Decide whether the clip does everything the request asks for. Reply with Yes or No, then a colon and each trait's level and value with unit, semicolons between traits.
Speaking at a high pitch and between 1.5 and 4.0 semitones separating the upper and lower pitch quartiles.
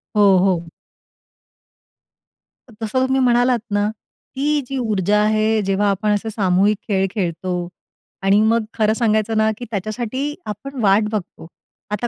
Yes: high, 215 Hz; average, 3.1 semitones